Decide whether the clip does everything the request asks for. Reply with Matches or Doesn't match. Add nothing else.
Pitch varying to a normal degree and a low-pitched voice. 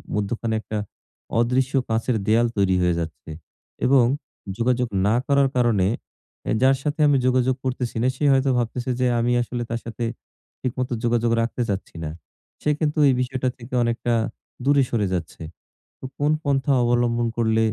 Doesn't match